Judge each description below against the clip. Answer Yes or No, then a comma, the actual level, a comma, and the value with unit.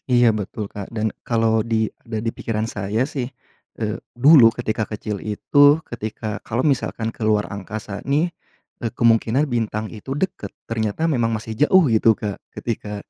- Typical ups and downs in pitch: No, narrow, 2.3 semitones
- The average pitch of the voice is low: Yes, low, 110 Hz